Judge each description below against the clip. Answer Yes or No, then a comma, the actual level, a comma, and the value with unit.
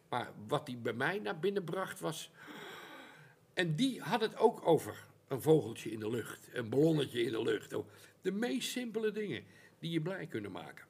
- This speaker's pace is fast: No, average, 185 wpm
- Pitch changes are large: Yes, wide, 7.8 semitones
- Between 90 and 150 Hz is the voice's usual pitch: No, medium, 180 Hz